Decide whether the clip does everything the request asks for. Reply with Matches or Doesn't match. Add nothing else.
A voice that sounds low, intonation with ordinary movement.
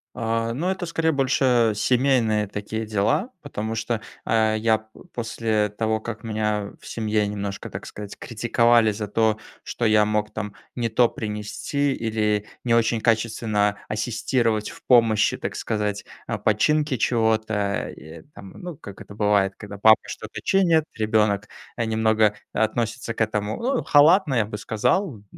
Doesn't match